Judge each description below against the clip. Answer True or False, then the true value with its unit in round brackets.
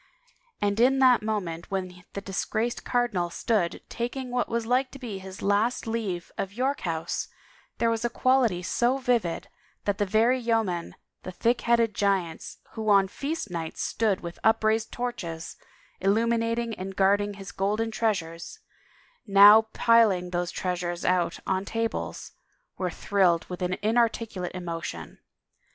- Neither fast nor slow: True (145 wpm)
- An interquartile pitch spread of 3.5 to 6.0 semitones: True (4.2 semitones)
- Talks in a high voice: True (205 Hz)